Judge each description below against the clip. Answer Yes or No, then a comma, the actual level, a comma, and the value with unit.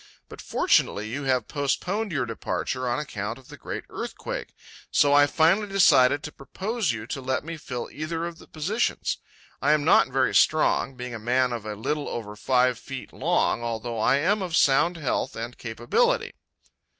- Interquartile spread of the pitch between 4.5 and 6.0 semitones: Yes, average, 4.9 semitones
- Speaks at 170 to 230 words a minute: Yes, average, 180 wpm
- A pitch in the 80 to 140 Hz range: Yes, low, 135 Hz